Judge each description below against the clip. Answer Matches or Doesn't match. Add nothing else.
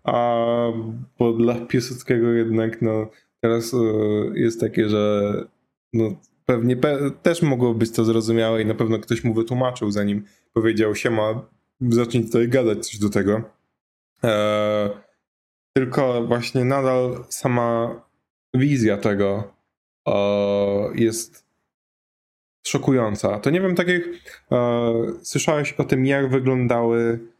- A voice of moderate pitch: Doesn't match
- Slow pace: Doesn't match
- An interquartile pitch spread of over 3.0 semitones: Doesn't match